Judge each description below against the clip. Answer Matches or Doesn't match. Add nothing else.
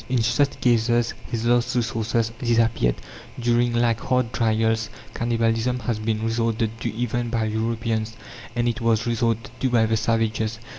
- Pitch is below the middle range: Matches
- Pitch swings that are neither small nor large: Doesn't match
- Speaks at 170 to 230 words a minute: Doesn't match